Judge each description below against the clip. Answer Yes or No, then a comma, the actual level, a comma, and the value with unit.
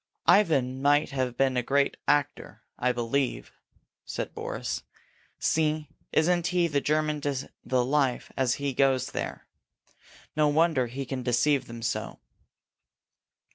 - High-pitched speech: No, medium, 140 Hz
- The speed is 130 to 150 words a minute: Yes, slow, 135 wpm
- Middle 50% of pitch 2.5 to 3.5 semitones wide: Yes, average, 2.9 semitones